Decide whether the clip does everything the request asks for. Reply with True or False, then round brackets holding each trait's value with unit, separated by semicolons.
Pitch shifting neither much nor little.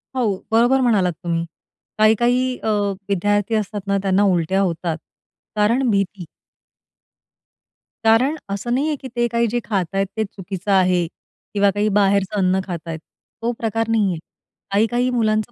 True (3.4 semitones)